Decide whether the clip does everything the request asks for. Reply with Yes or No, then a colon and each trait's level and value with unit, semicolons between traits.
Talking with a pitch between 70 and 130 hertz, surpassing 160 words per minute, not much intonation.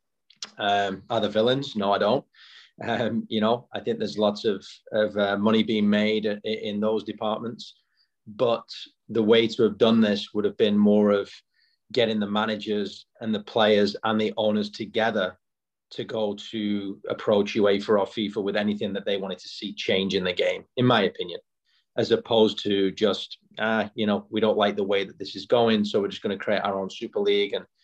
Yes: low, 105 Hz; average, 200 wpm; narrow, 1.4 semitones